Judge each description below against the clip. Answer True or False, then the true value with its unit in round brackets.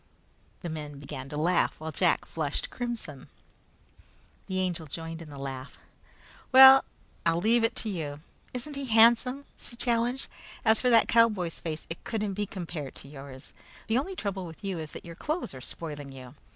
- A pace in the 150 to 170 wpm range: False (180 wpm)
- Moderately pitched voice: True (175 Hz)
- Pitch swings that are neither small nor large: False (7.4 semitones)